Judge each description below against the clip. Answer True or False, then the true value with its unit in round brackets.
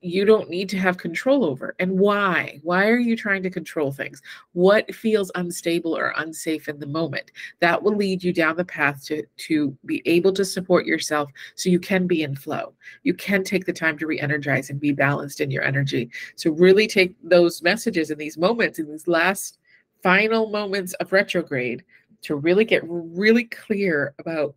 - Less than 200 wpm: True (190 wpm)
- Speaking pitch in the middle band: True (180 Hz)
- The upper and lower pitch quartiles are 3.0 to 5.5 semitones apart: True (4.0 semitones)